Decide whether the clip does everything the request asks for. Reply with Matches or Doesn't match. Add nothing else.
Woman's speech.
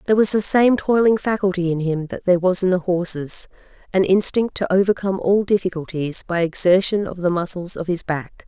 Matches